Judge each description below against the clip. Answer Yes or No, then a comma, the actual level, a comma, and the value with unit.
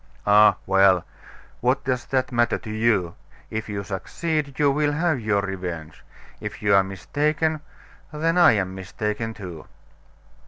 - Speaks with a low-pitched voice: Yes, low, 110 Hz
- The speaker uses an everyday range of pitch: No, wide, 6.7 semitones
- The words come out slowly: No, average, 145 wpm